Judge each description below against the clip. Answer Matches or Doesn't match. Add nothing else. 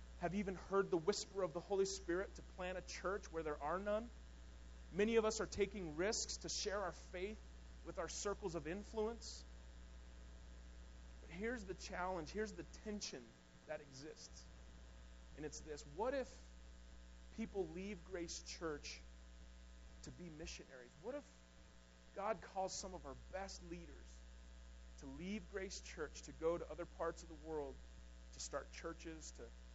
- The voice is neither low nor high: Matches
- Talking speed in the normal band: Matches